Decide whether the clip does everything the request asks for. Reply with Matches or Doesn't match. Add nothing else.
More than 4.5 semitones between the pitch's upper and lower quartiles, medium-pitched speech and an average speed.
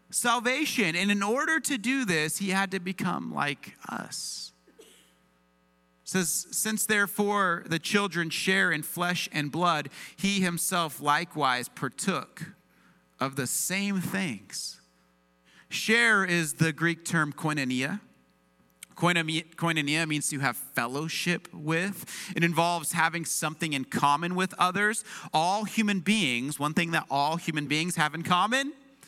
Doesn't match